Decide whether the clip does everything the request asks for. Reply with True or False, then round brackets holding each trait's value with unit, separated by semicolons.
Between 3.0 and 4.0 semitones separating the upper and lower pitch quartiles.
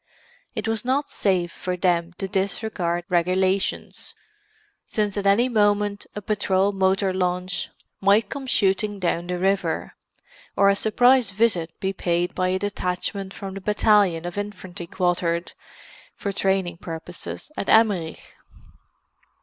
False (2.5 semitones)